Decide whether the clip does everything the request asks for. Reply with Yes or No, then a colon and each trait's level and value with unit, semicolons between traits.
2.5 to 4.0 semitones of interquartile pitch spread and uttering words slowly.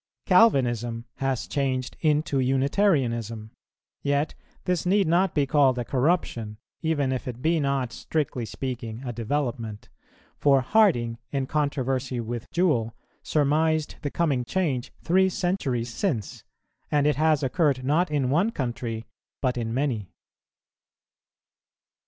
No: average, 4.4 semitones; slow, 125 wpm